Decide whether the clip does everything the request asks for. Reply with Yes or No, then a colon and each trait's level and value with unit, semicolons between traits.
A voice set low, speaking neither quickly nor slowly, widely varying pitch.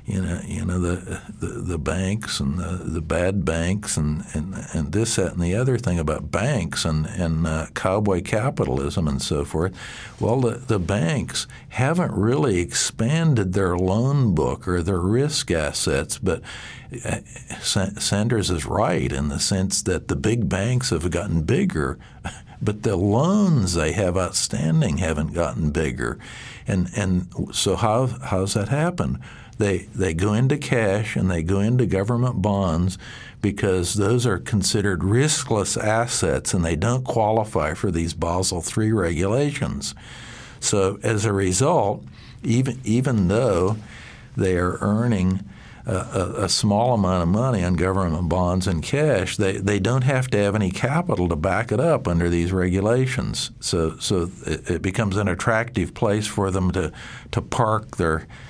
No: very low, 95 Hz; average, 155 wpm; average, 4.4 semitones